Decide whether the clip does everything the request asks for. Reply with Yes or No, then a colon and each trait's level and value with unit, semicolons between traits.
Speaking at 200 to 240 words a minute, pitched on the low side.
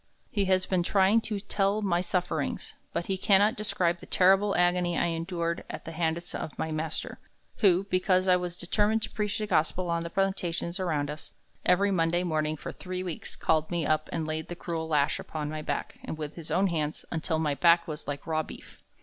No: fast, 205 wpm; medium, 175 Hz